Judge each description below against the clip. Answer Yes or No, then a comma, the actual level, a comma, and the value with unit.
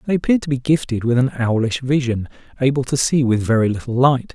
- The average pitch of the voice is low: Yes, low, 130 Hz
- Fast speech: Yes, fast, 220 wpm